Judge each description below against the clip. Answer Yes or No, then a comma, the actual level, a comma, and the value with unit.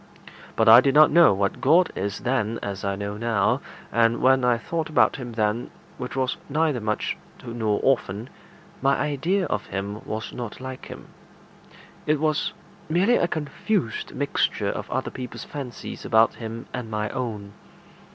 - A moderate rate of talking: Yes, average, 160 wpm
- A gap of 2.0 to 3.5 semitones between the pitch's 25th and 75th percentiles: No, average, 4.9 semitones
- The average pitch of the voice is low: Yes, low, 120 Hz